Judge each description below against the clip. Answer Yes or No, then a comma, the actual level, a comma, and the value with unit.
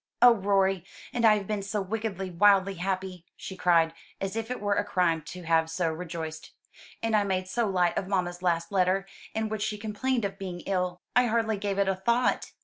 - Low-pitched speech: No, high, 195 Hz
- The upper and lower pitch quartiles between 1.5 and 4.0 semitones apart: Yes, average, 2.8 semitones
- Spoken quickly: Yes, fast, 210 wpm